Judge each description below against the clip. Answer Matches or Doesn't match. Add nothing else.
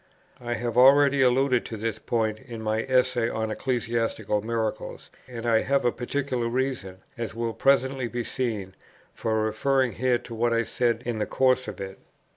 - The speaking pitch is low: Matches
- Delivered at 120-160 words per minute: Doesn't match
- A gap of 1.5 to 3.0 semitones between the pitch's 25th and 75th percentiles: Matches